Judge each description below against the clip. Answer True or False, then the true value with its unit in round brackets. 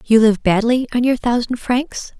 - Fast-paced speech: False (190 wpm)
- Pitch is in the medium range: False (235 Hz)